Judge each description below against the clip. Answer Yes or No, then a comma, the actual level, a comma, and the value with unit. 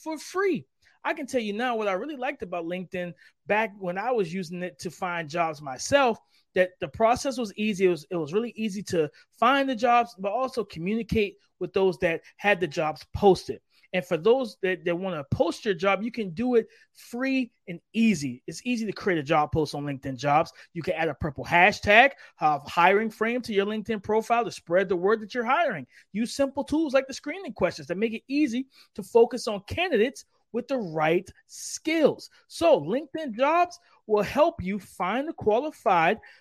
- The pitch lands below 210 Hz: No, high, 215 Hz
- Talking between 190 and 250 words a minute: Yes, fast, 205 wpm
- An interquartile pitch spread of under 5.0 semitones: No, wide, 5.6 semitones